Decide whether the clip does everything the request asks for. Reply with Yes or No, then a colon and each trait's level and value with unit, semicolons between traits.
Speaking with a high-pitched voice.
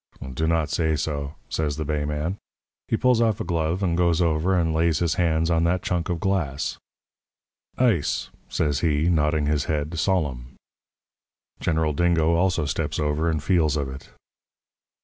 No: very low, 80 Hz